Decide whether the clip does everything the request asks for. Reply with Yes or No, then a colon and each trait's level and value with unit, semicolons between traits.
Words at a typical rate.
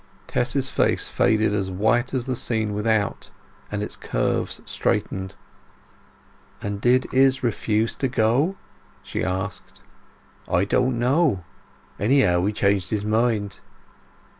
No: slow, 120 wpm